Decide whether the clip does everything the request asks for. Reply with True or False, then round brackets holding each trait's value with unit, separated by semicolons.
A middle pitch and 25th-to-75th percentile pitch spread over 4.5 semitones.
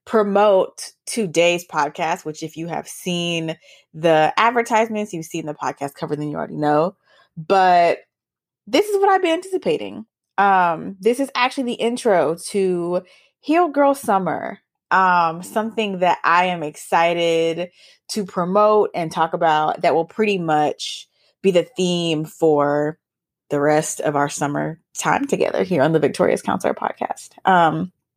True (175 Hz; 4.9 semitones)